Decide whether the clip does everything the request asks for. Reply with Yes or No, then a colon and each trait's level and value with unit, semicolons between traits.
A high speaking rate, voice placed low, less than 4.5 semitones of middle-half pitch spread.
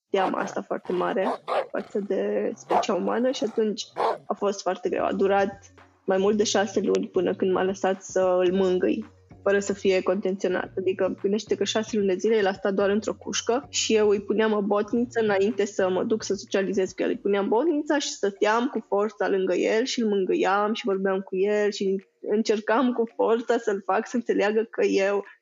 No: fast, 200 wpm; high, 200 Hz; narrow, 2.4 semitones